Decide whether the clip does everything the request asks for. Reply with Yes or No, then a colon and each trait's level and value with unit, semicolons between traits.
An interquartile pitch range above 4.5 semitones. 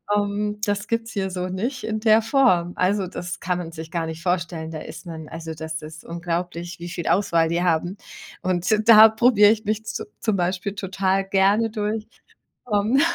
No: average, 3.6 semitones